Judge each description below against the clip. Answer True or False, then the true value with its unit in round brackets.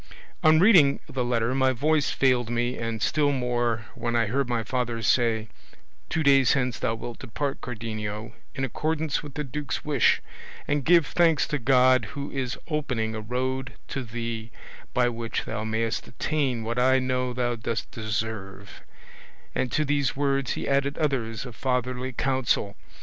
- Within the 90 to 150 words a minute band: False (165 wpm)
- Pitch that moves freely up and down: False (3.3 semitones)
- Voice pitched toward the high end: False (125 Hz)